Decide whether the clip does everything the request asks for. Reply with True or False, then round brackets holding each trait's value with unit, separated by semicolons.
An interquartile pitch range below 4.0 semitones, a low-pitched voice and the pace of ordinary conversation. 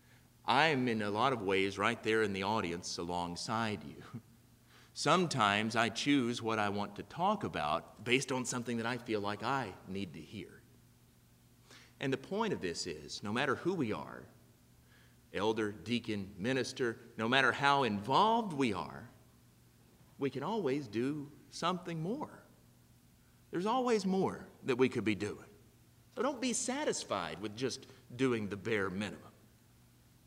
False (4.7 semitones; 115 Hz; 155 wpm)